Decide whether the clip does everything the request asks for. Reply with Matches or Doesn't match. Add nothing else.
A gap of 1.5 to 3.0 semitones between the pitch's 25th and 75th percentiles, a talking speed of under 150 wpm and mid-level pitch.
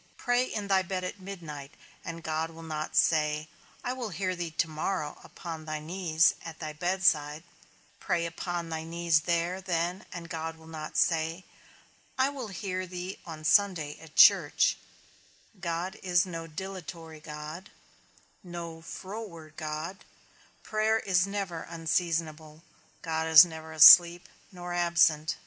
Matches